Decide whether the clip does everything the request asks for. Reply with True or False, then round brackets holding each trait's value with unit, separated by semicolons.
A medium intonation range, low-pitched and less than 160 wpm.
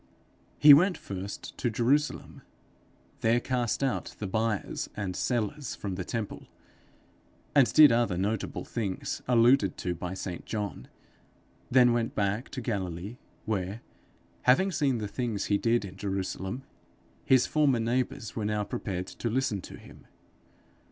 True (4.1 semitones; 115 Hz; 140 wpm)